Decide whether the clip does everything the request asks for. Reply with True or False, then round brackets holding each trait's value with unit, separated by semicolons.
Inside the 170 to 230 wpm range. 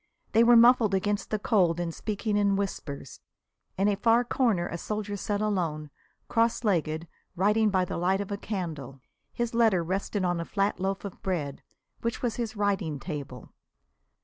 True (175 wpm)